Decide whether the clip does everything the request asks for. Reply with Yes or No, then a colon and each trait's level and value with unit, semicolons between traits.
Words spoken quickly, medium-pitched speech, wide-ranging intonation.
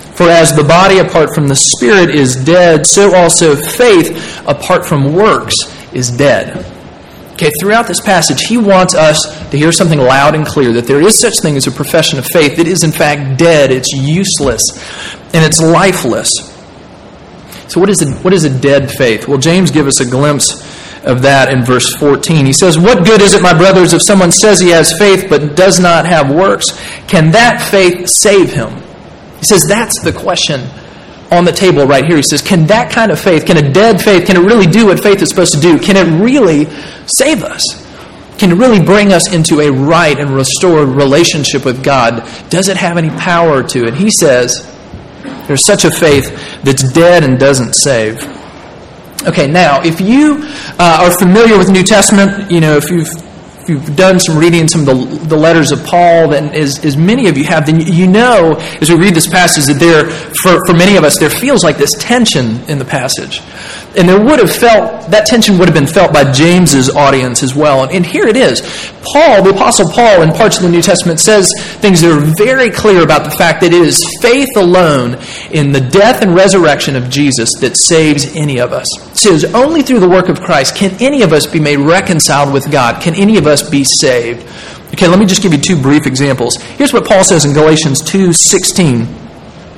No: fast, 210 wpm; medium, 165 Hz; average, 4.7 semitones